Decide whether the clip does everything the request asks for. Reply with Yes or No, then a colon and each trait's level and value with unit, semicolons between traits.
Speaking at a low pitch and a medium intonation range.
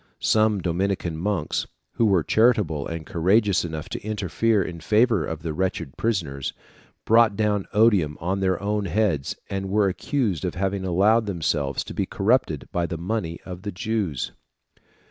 Yes: very low, 95 Hz; average, 4.1 semitones